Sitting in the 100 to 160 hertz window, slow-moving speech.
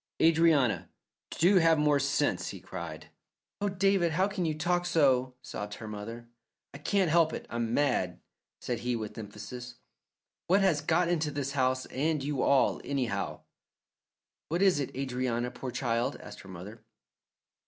No: medium, 140 Hz; average, 155 wpm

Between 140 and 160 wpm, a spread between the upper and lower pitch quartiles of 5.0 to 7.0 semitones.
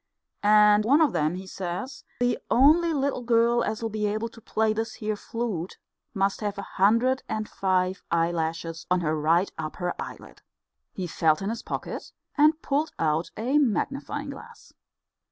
Yes: average, 155 wpm; wide, 5.5 semitones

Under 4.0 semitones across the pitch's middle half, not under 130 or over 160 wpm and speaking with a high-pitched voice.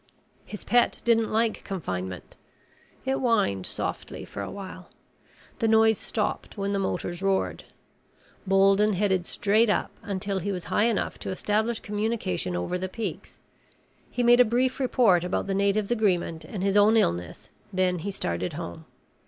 Yes: average, 3.4 semitones; average, 155 wpm; high, 200 Hz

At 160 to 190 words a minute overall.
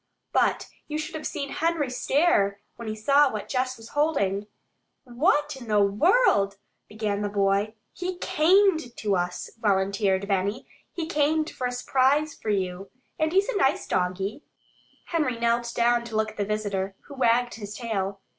Yes: average, 170 wpm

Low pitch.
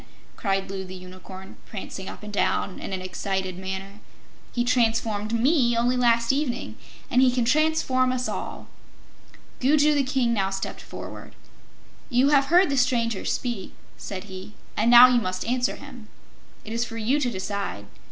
No: high, 230 Hz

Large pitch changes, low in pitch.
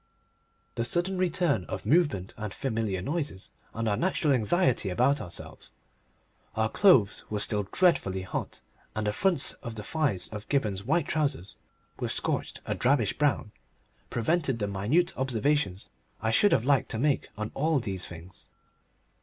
Yes: wide, 6.6 semitones; low, 115 Hz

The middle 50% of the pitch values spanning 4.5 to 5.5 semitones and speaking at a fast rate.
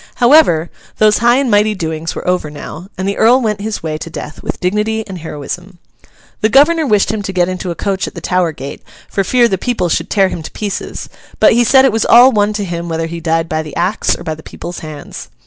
Yes: average, 4.9 semitones; fast, 245 wpm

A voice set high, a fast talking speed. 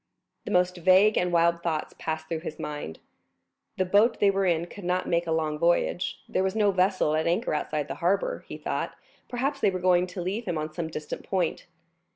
No: medium, 175 Hz; fast, 210 wpm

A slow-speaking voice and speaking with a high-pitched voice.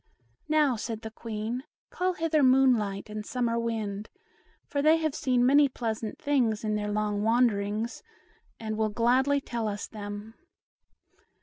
No: average, 145 wpm; high, 230 Hz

